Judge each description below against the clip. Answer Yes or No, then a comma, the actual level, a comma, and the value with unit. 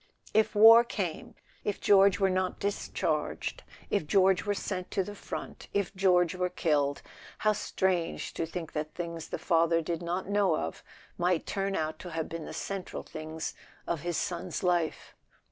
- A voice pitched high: No, medium, 180 Hz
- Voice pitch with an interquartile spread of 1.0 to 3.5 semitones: Yes, average, 3.0 semitones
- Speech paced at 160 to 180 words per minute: Yes, average, 170 wpm